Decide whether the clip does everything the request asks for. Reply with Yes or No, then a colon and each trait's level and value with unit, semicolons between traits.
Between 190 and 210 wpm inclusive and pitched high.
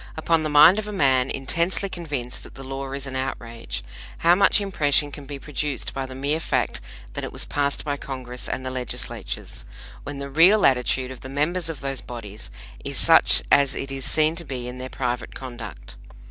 No: average, 200 wpm; low, 135 Hz